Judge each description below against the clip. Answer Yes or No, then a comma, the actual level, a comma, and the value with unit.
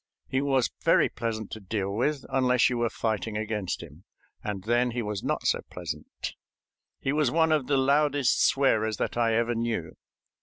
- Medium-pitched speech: No, low, 120 Hz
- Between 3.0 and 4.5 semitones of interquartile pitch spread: Yes, average, 3.6 semitones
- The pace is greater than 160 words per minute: Yes, average, 180 wpm